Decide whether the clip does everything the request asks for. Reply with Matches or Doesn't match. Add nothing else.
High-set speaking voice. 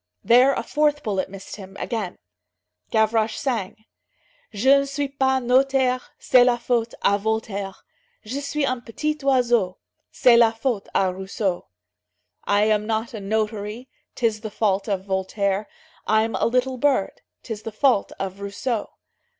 Matches